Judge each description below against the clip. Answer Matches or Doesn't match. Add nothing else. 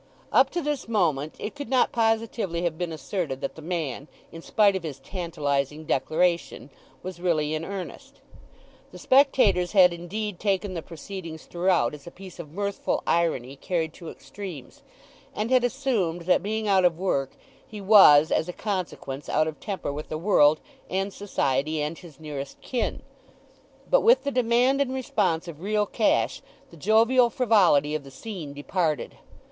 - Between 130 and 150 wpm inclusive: Doesn't match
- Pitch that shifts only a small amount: Doesn't match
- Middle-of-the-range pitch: Matches